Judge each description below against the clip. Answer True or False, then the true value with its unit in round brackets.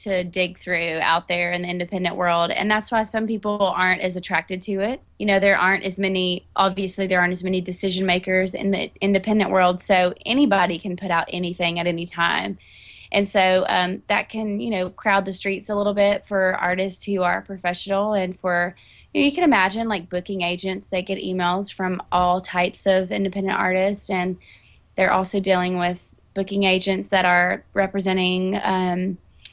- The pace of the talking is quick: False (190 wpm)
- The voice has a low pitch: False (185 Hz)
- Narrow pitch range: True (1.7 semitones)